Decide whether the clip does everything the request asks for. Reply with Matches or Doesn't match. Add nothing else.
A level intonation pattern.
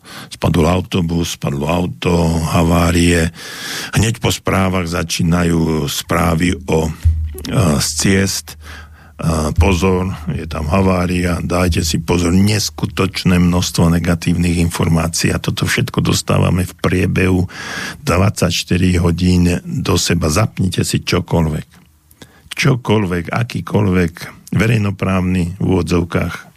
Matches